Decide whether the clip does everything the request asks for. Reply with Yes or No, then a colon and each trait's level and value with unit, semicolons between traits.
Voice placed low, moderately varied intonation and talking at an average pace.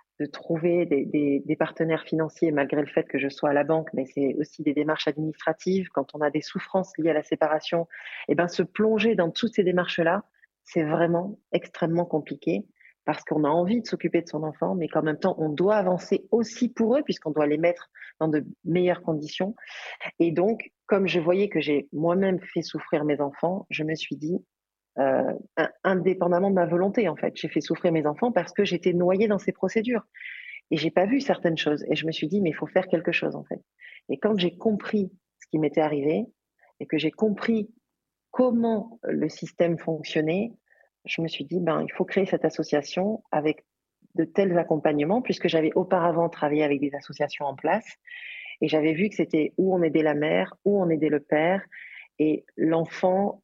No: medium, 170 Hz; average, 3.8 semitones; average, 205 wpm